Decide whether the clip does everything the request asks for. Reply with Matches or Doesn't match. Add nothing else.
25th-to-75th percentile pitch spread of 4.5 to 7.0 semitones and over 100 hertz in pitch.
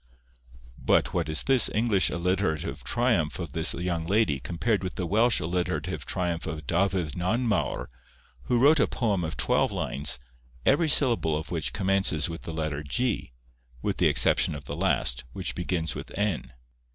Doesn't match